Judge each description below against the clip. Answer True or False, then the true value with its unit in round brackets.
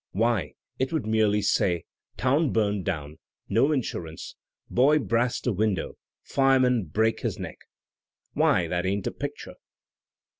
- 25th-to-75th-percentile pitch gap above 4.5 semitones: True (5.5 semitones)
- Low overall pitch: True (110 Hz)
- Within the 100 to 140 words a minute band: True (135 wpm)